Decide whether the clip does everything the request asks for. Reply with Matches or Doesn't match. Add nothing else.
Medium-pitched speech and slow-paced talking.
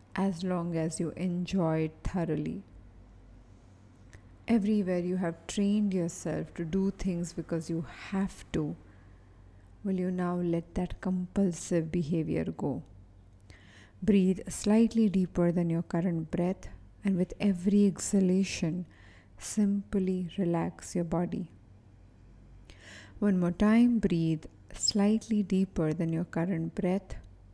Matches